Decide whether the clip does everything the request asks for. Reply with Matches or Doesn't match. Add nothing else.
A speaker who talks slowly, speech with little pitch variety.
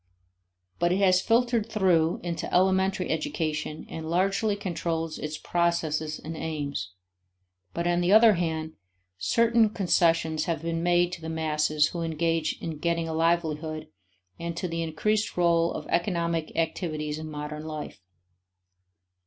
Doesn't match